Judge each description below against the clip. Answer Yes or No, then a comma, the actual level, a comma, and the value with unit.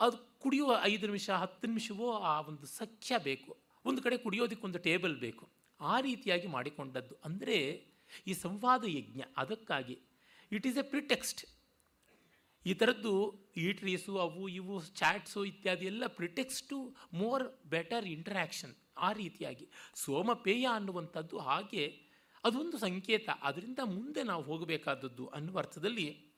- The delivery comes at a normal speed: No, fast, 125 wpm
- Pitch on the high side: Yes, high, 195 Hz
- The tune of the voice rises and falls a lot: Yes, wide, 5.8 semitones